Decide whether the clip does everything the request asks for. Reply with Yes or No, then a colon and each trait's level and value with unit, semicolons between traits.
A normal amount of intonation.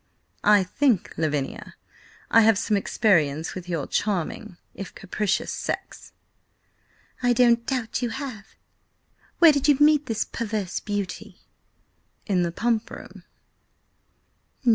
Yes: average, 4.7 semitones